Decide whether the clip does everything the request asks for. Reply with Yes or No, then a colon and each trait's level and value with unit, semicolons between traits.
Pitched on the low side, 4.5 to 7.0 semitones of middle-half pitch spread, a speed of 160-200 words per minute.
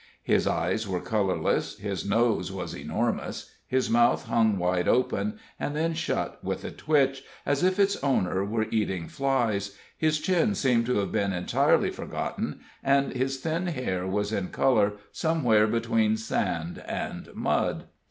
No: low, 115 Hz; wide, 5.6 semitones; average, 150 wpm